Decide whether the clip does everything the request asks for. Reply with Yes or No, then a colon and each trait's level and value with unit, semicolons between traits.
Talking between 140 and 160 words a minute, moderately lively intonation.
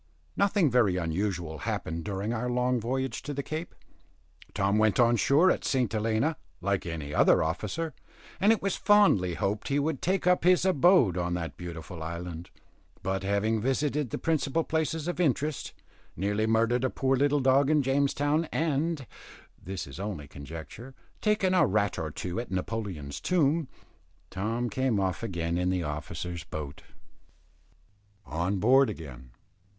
No: average, 155 wpm; wide, 8.2 semitones